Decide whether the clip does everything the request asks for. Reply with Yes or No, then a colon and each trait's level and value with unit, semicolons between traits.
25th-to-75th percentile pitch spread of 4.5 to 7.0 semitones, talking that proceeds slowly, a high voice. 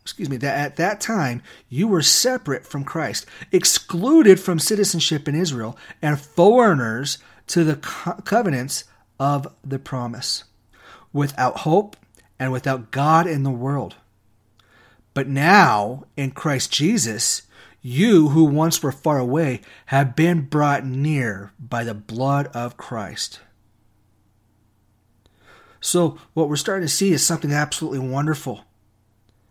No: average, 5.2 semitones; slow, 125 wpm; medium, 140 Hz